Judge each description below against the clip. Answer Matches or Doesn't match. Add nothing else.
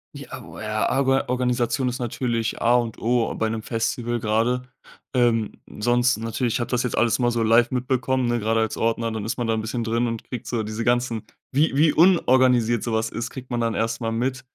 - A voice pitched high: Doesn't match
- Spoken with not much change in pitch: Matches